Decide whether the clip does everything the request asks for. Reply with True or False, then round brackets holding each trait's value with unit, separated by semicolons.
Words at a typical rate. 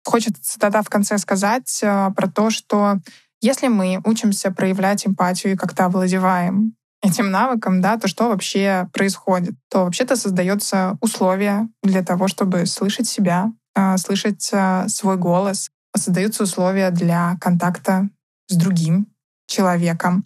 True (125 wpm)